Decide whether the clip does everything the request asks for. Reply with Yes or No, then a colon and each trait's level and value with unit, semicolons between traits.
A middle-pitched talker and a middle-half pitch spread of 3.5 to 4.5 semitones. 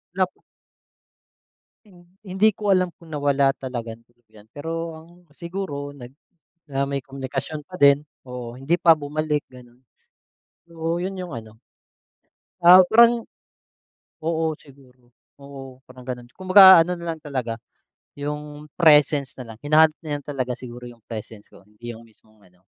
No: medium, 145 Hz; average, 4.9 semitones